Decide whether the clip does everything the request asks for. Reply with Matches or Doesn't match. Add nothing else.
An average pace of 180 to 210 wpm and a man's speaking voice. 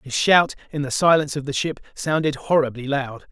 Matches